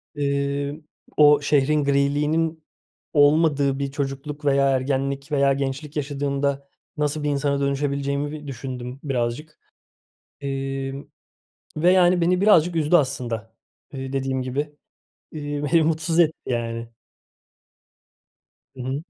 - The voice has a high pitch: No, medium, 140 Hz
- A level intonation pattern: Yes, narrow, 1.7 semitones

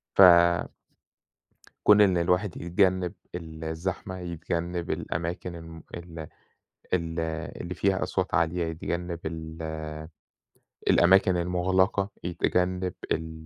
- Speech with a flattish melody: Yes, narrow, 1.9 semitones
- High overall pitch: No, very low, 85 Hz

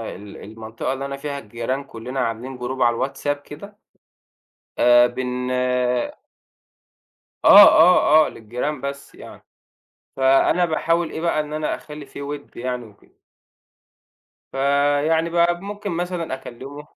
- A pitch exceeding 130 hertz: Yes, medium, 140 Hz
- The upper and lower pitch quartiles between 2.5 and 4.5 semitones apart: Yes, average, 4.0 semitones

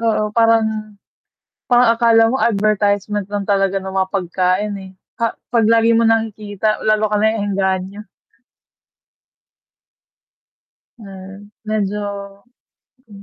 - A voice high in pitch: Yes, high, 210 Hz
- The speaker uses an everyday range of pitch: No, narrow, 2.3 semitones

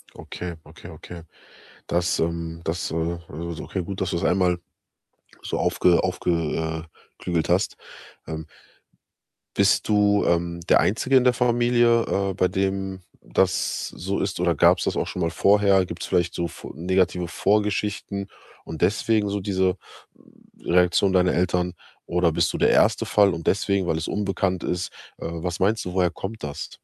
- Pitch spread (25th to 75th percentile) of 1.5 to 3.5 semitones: Yes, narrow, 2.6 semitones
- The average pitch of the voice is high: No, very low, 90 Hz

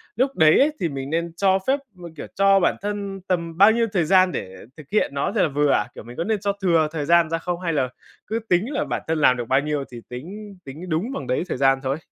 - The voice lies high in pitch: No, medium, 170 Hz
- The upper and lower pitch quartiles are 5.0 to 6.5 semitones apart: Yes, wide, 5.4 semitones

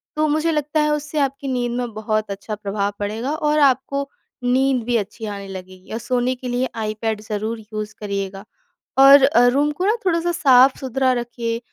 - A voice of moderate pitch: No, high, 245 Hz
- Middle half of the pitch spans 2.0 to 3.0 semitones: No, average, 4.5 semitones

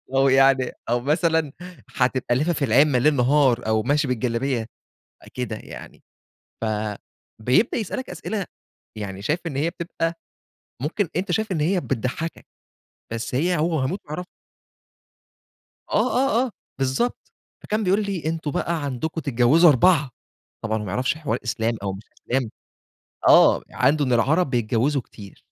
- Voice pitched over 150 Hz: No, medium, 140 Hz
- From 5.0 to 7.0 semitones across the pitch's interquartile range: Yes, average, 5.3 semitones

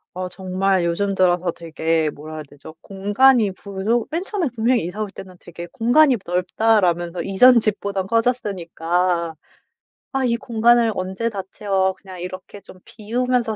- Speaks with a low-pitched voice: No, high, 195 Hz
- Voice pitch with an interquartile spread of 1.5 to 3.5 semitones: No, average, 4.3 semitones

